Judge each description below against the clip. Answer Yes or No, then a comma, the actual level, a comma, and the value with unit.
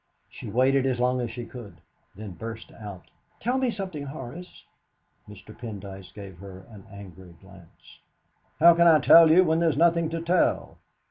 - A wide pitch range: Yes, wide, 8.7 semitones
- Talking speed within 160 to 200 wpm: Yes, average, 170 wpm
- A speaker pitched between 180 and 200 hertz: No, low, 125 Hz